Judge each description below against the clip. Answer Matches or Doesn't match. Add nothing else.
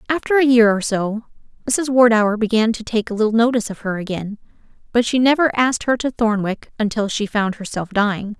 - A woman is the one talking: Matches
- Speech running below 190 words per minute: Doesn't match